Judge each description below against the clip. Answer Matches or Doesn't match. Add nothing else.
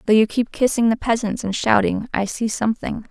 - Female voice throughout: Matches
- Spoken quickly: Matches